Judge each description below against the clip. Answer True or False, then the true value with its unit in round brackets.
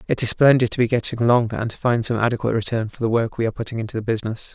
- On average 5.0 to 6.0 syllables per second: False (7.8 syllables/s)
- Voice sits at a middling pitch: False (115 Hz)